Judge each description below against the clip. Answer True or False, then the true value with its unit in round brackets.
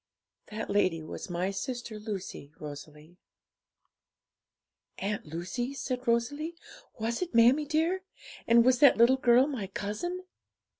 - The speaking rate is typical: False (120 wpm)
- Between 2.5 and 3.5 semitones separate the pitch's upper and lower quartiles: False (5.5 semitones)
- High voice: True (235 Hz)